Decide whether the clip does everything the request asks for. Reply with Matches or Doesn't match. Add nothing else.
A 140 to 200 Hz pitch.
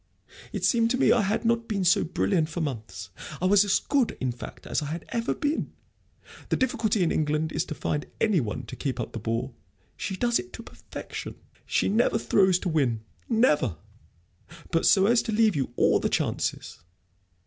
Matches